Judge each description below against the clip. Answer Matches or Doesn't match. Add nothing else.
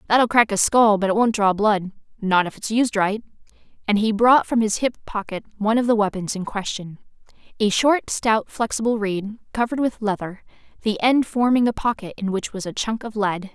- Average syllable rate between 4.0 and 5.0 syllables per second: Doesn't match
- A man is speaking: Doesn't match